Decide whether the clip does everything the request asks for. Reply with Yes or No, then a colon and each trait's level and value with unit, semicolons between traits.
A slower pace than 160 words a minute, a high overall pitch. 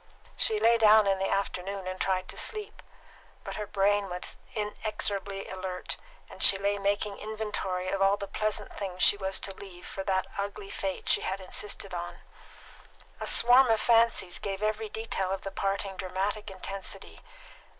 No: average, 170 wpm; high, 195 Hz